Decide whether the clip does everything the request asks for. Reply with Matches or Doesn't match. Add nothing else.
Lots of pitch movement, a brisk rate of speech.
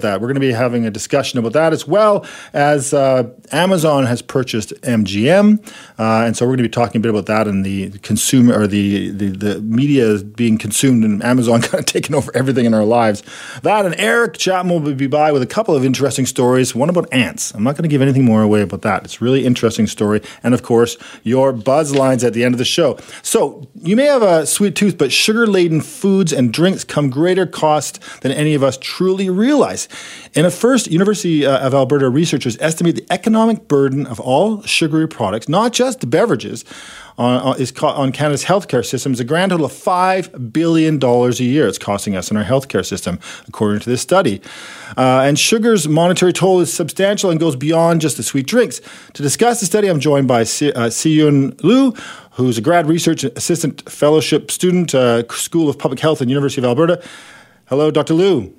Matches